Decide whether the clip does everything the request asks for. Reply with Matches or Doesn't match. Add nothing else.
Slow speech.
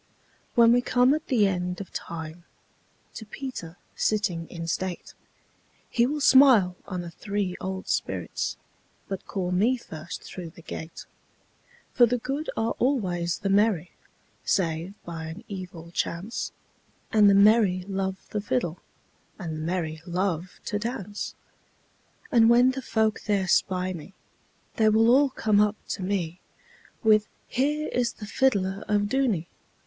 Matches